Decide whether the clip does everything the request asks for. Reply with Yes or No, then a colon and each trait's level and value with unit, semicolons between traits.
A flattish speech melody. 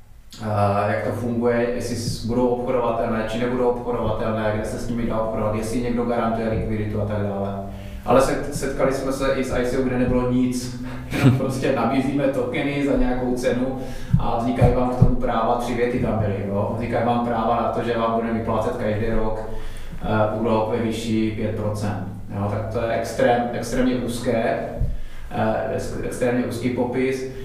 Yes: narrow, 2.2 semitones